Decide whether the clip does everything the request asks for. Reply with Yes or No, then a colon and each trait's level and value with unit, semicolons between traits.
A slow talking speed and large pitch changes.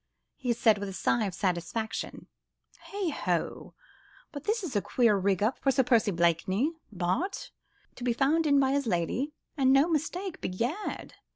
No: average, 170 wpm; wide, 6.6 semitones